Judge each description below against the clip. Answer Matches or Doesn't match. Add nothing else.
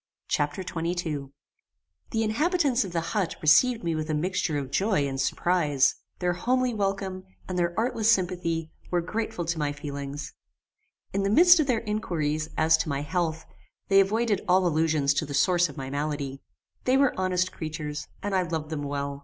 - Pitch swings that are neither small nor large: Matches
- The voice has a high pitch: Doesn't match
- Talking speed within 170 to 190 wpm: Matches